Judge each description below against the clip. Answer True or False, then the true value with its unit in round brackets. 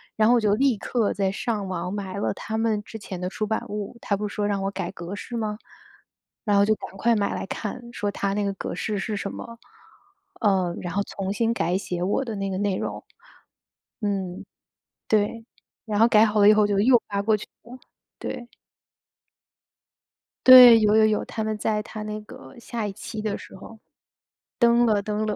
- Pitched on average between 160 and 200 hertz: False (210 Hz)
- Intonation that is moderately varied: False (1.9 semitones)